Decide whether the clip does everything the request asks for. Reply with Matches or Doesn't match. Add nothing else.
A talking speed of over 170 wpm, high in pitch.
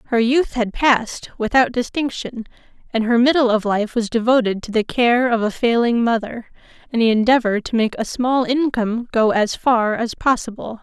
Matches